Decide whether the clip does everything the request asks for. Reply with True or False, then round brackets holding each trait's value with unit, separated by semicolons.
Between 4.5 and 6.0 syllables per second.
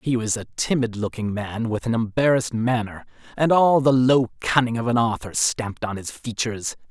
True (5.3 syllables/s)